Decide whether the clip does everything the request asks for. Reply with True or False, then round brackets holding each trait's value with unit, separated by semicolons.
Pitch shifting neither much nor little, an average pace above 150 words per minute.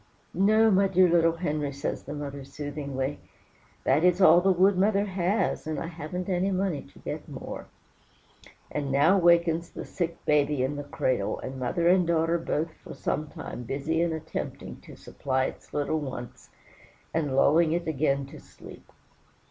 True (3.9 semitones; 170 wpm)